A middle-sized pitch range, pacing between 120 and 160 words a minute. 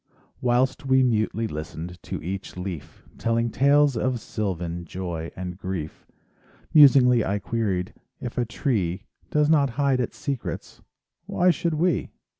No: wide, 6.5 semitones; slow, 135 wpm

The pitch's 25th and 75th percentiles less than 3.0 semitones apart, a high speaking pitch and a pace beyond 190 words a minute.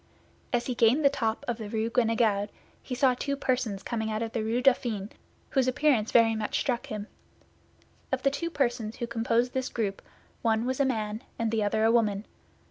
Yes: narrow, 2.6 semitones; high, 230 Hz; average, 200 wpm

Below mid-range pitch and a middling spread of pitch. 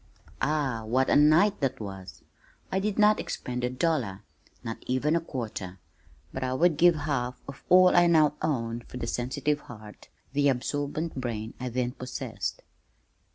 Yes: low, 130 Hz; average, 4.2 semitones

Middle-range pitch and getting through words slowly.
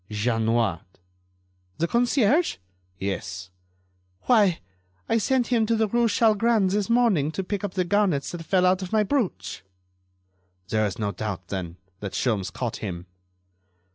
No: medium, 180 Hz; average, 145 wpm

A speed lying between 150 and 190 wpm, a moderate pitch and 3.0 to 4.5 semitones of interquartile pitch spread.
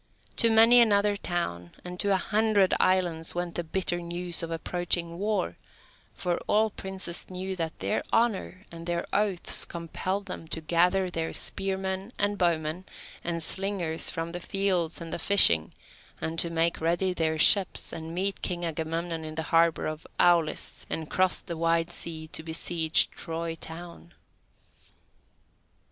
No: average, 155 wpm; medium, 175 Hz; narrow, 2.6 semitones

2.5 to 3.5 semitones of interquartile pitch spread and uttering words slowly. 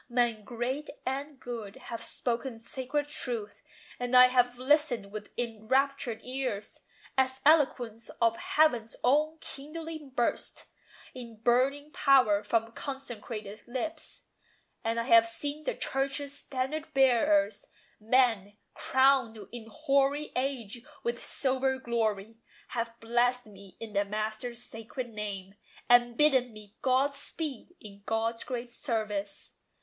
Yes: average, 3.2 semitones; slow, 125 wpm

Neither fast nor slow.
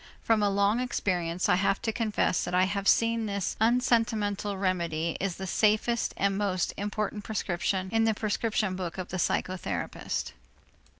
Yes: average, 165 wpm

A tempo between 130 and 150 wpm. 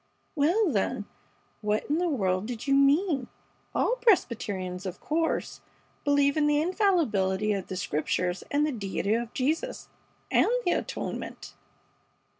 Yes: slow, 135 wpm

